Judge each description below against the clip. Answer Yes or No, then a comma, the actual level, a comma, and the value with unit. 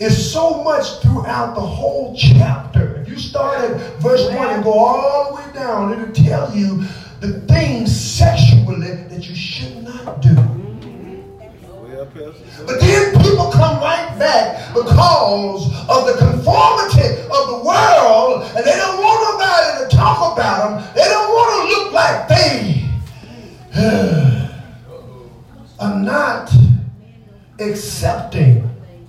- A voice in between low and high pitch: Yes, medium, 165 Hz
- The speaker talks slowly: Yes, slow, 130 wpm